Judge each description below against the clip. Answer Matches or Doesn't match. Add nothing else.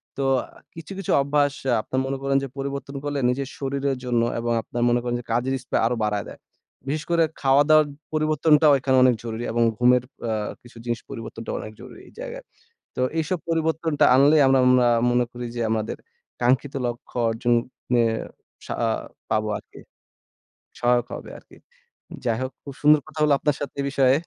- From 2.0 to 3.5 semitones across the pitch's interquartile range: Matches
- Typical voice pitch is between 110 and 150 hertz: Matches